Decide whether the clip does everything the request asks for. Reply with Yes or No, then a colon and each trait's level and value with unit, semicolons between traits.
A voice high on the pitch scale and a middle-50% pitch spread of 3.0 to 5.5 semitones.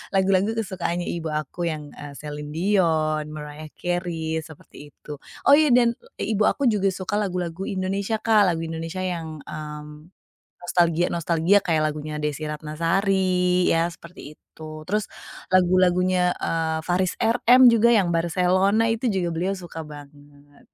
No: medium, 175 Hz; average, 3.6 semitones